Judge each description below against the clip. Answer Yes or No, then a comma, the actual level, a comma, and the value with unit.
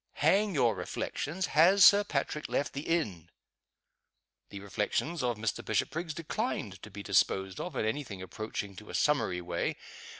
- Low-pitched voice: Yes, low, 125 Hz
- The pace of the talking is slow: No, average, 160 wpm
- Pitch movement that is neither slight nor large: No, wide, 8.5 semitones